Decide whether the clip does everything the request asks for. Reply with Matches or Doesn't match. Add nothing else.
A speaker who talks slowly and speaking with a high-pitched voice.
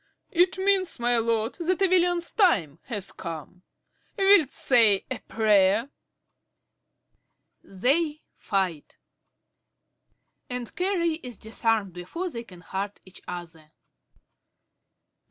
Matches